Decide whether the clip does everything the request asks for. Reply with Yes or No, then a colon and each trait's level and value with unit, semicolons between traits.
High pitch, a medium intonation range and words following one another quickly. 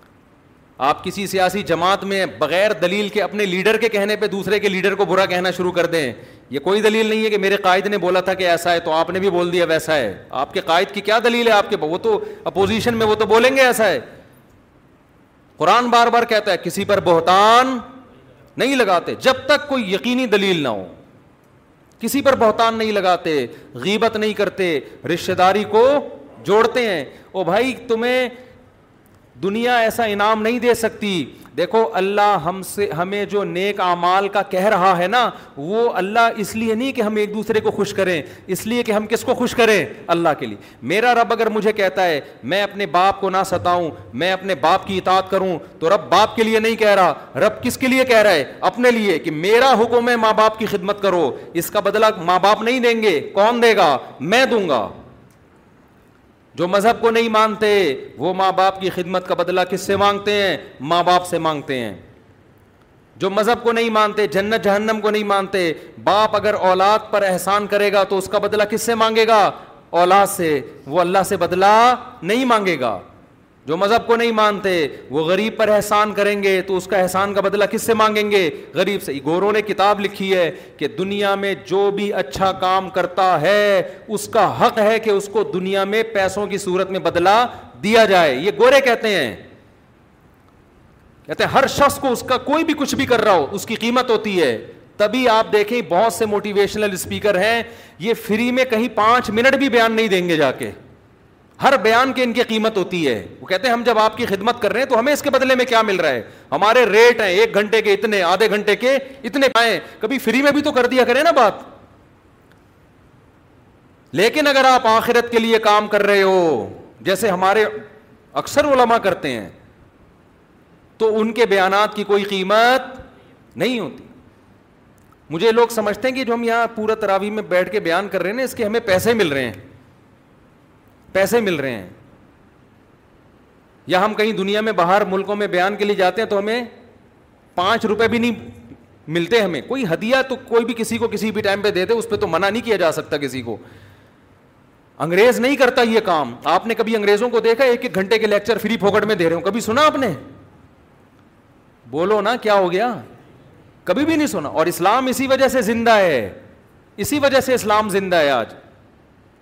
Yes: high, 210 Hz; average, 3.6 semitones; fast, 205 wpm